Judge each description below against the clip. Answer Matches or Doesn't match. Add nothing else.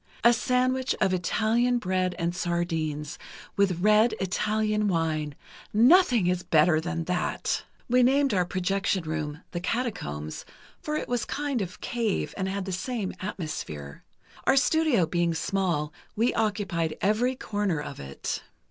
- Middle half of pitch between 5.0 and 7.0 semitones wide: Matches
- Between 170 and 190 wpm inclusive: Doesn't match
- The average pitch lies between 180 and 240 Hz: Matches